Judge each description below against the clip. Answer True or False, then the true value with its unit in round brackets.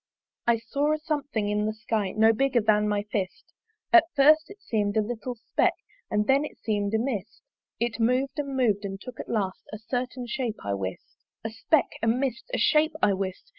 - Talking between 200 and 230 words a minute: True (205 wpm)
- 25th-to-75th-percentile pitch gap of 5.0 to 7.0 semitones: False (4.6 semitones)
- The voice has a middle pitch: False (230 Hz)